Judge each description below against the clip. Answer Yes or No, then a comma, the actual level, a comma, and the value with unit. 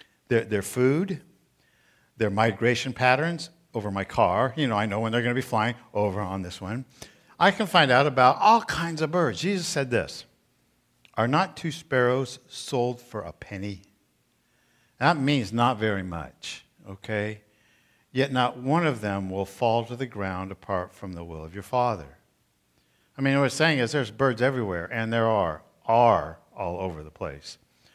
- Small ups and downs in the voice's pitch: No, average, 5.1 semitones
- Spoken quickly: No, average, 175 wpm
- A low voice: Yes, low, 120 Hz